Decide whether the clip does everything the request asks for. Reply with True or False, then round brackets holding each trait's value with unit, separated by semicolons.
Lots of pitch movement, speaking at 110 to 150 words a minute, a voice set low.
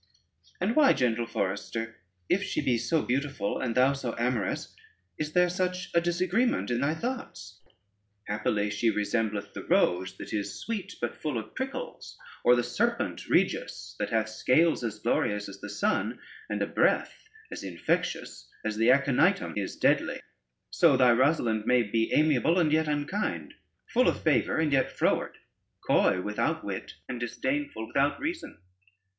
False (6.6 semitones; 160 wpm; 125 Hz)